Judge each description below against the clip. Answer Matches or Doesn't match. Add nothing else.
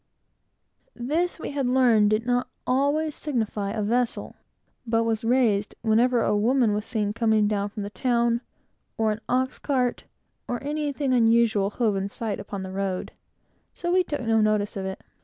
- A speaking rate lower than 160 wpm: Doesn't match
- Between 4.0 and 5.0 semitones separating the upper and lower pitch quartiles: Doesn't match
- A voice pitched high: Matches